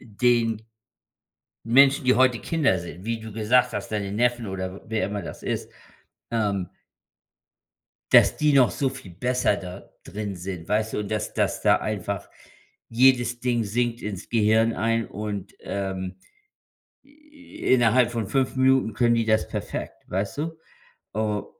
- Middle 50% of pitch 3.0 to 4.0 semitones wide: Yes, average, 3.6 semitones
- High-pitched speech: No, low, 110 Hz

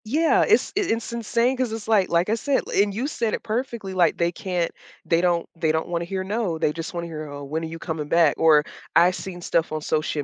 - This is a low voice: No, medium, 175 Hz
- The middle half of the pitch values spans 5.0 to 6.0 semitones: Yes, average, 5.3 semitones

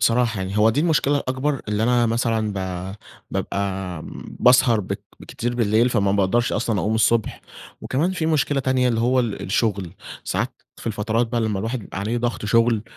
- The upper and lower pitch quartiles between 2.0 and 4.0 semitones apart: Yes, average, 3.1 semitones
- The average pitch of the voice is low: Yes, low, 115 Hz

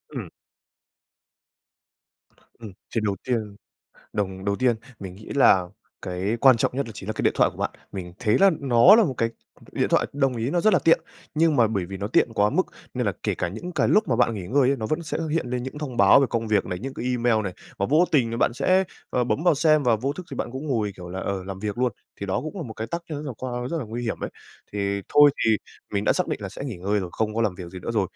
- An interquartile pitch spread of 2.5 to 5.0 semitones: No, wide, 5.5 semitones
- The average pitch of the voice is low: Yes, low, 115 Hz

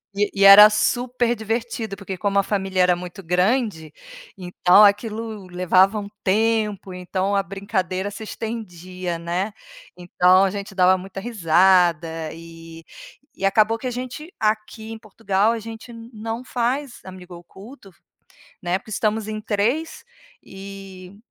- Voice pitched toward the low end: No, high, 200 Hz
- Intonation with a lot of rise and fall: No, average, 3.3 semitones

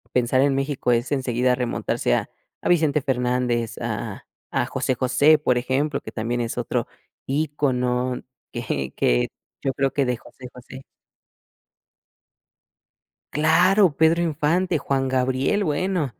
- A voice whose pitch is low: Yes, low, 130 Hz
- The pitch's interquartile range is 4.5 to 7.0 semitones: No, average, 3.3 semitones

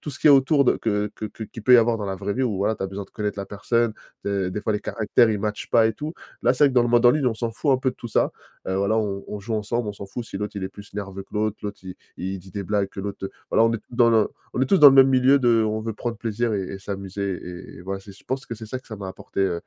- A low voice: Yes, low, 110 Hz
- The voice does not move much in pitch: No, average, 3.3 semitones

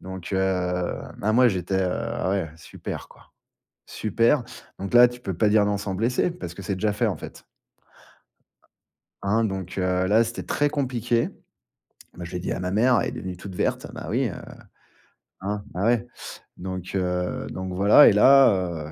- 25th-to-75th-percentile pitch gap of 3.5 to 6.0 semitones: Yes, average, 3.9 semitones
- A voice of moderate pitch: No, low, 100 Hz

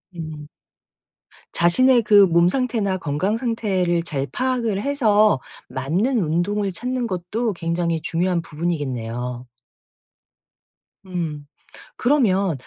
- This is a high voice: No, medium, 180 Hz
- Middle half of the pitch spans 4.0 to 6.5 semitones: Yes, average, 5.3 semitones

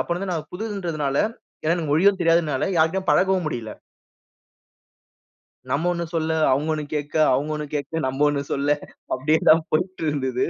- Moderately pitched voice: Yes, medium, 155 Hz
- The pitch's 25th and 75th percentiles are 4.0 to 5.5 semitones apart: No, average, 3.1 semitones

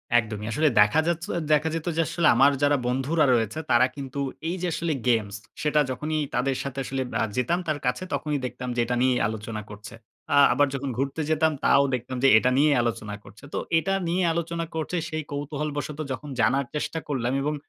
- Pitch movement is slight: No, average, 4.0 semitones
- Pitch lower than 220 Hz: Yes, medium, 140 Hz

